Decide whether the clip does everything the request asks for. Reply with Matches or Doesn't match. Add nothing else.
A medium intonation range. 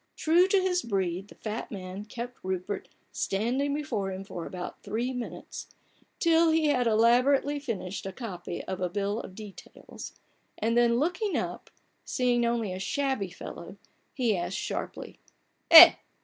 Doesn't match